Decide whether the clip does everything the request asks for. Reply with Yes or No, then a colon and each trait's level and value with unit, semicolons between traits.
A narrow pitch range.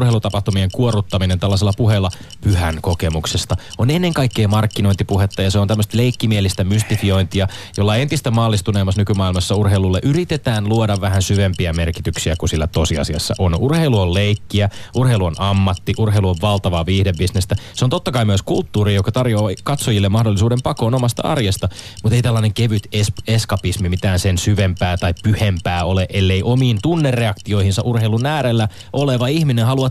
No: average, 3.1 semitones